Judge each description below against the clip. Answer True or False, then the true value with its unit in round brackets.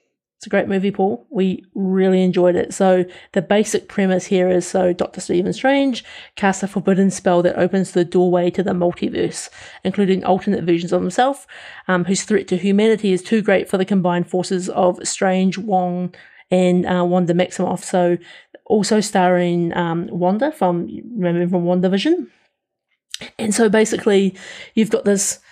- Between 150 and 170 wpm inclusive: True (160 wpm)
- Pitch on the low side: False (190 Hz)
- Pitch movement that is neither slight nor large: False (2.0 semitones)